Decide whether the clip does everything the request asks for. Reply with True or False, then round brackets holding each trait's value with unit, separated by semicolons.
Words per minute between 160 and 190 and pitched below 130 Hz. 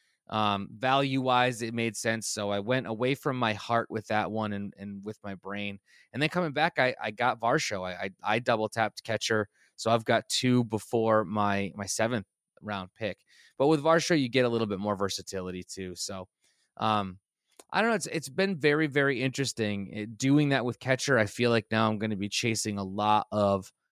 False (205 wpm; 110 Hz)